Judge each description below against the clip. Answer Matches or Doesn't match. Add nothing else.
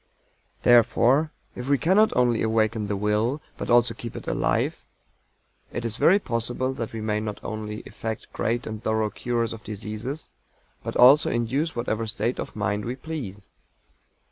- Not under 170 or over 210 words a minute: Doesn't match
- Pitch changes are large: Doesn't match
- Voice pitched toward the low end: Matches